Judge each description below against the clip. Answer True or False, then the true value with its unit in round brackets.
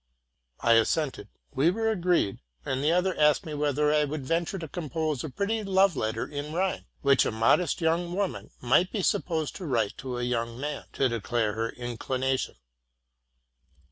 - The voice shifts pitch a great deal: True (5.8 semitones)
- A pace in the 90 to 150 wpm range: False (175 wpm)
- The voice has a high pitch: False (150 Hz)